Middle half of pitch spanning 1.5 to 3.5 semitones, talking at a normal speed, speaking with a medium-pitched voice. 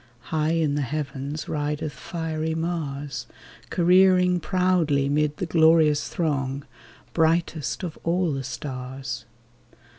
No: average, 2.9 semitones; slow, 110 wpm; medium, 155 Hz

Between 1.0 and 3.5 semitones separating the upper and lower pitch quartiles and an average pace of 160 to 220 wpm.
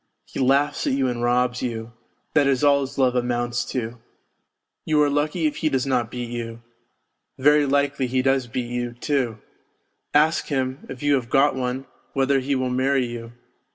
Yes: narrow, 2.5 semitones; average, 185 wpm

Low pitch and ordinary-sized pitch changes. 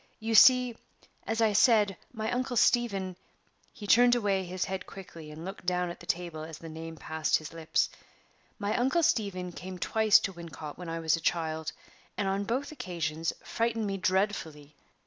No: high, 190 Hz; average, 5.0 semitones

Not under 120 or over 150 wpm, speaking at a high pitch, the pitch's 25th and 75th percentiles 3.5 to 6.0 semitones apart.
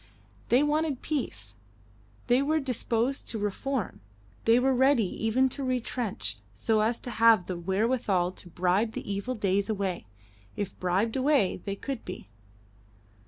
Yes: average, 145 wpm; high, 225 Hz; average, 5.1 semitones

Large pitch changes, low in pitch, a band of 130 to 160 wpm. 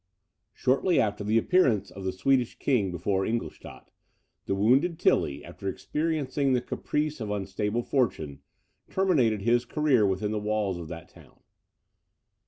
Yes: wide, 5.7 semitones; low, 110 Hz; average, 140 wpm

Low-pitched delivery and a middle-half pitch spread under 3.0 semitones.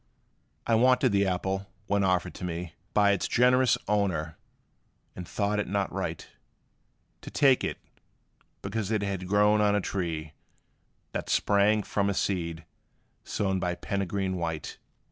Yes: low, 100 Hz; narrow, 2.5 semitones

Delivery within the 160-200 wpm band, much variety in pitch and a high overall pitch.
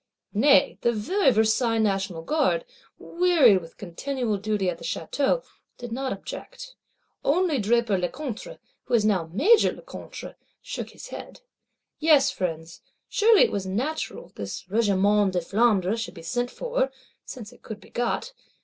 No: average, 145 wpm; wide, 6.8 semitones; high, 230 Hz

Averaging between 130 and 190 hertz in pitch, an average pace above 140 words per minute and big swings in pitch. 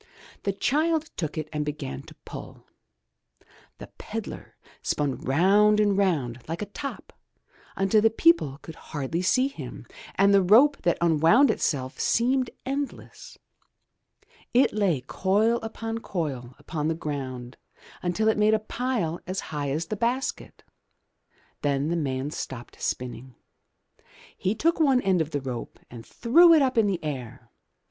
Yes: medium, 185 Hz; average, 150 wpm; wide, 7.7 semitones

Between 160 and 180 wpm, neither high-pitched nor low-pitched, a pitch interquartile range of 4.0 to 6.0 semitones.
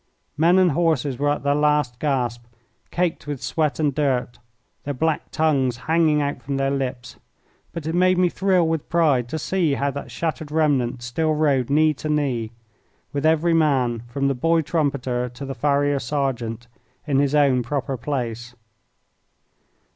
No: average, 165 wpm; medium, 145 Hz; average, 3.6 semitones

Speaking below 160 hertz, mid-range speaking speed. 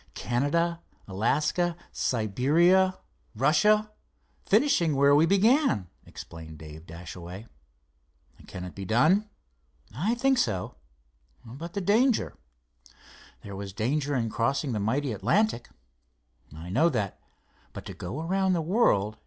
No: medium, 140 Hz; slow, 115 wpm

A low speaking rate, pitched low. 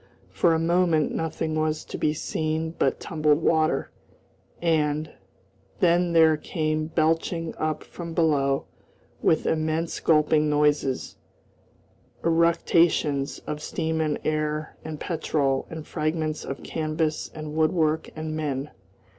No: slow, 120 wpm; medium, 155 Hz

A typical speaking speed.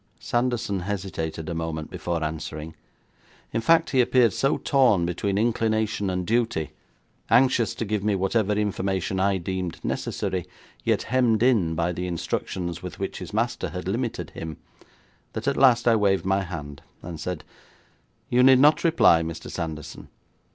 Yes: average, 155 wpm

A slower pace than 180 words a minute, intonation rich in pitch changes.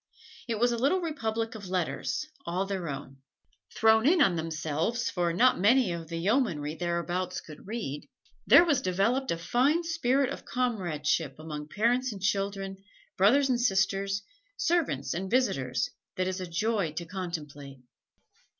Yes: average, 150 wpm; wide, 6.4 semitones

